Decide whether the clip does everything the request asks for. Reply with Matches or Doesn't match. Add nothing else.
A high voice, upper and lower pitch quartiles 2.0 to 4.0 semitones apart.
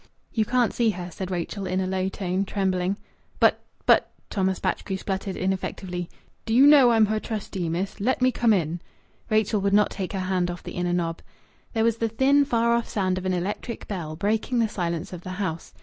Matches